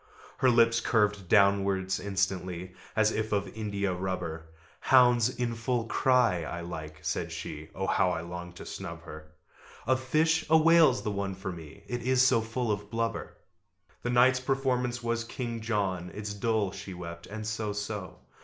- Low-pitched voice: Yes, low, 105 Hz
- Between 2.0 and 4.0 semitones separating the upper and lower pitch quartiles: No, average, 4.7 semitones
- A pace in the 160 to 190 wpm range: Yes, average, 170 wpm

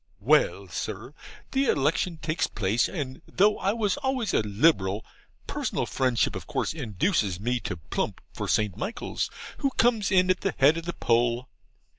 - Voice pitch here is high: No, medium, 150 Hz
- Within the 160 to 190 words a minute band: Yes, average, 165 wpm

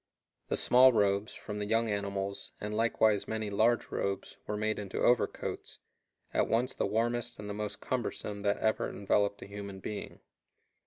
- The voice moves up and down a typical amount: No, narrow, 2.0 semitones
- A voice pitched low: Yes, low, 105 Hz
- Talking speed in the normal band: Yes, average, 165 wpm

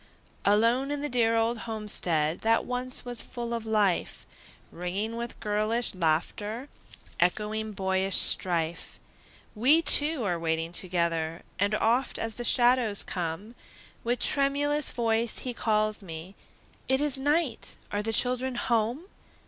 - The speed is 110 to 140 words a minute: Yes, slow, 135 wpm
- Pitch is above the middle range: Yes, high, 225 Hz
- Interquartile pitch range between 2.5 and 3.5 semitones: No, average, 4.6 semitones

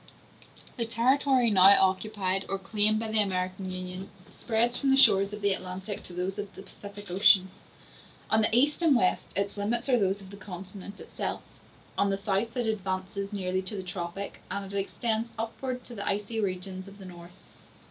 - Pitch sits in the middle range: No, high, 200 Hz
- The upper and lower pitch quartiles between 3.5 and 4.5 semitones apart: No, average, 2.7 semitones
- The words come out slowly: No, average, 190 wpm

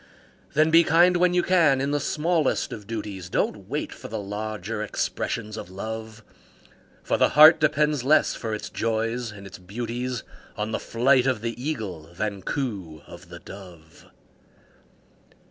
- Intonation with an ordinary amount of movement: No, wide, 5.7 semitones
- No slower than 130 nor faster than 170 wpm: Yes, average, 160 wpm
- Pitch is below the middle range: Yes, low, 115 Hz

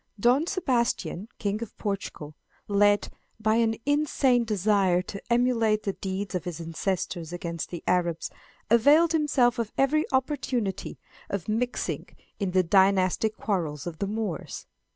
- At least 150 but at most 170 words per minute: No, slow, 135 wpm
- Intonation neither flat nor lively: Yes, average, 4.7 semitones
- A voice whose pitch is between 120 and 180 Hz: No, high, 205 Hz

